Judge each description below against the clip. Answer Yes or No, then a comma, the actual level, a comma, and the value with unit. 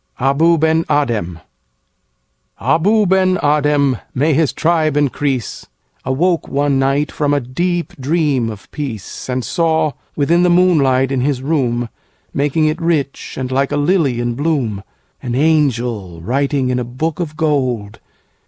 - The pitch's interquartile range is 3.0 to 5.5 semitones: Yes, average, 3.9 semitones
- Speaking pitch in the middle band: Yes, medium, 145 Hz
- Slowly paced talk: Yes, slow, 125 wpm